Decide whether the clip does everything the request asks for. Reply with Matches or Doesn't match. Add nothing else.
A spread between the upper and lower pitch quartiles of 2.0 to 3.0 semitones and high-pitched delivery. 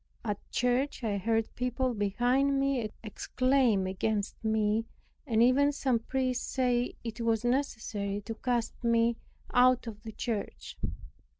Matches